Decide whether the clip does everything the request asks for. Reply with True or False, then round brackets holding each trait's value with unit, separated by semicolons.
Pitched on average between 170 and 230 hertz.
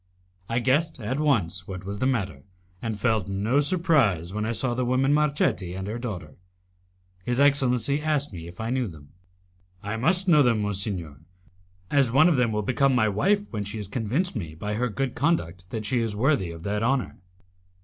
False (115 Hz)